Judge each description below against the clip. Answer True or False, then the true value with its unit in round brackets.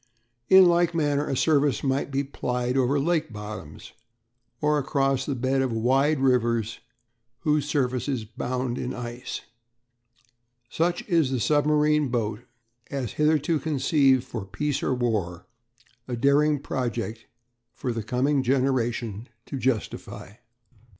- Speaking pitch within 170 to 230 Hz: False (130 Hz)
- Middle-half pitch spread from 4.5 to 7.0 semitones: False (3.5 semitones)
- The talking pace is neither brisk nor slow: False (130 wpm)